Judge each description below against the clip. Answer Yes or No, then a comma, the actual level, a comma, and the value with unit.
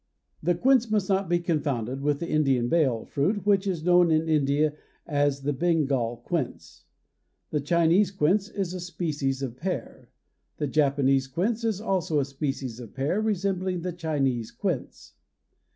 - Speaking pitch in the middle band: Yes, medium, 155 Hz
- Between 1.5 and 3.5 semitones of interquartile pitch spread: No, average, 5.0 semitones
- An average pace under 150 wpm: No, average, 155 wpm